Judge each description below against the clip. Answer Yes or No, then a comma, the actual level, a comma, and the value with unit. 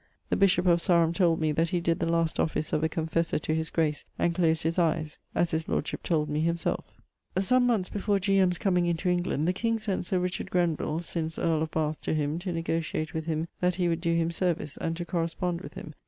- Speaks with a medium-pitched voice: Yes, medium, 170 Hz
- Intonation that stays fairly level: Yes, narrow, 1.9 semitones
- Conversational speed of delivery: No, fast, 235 wpm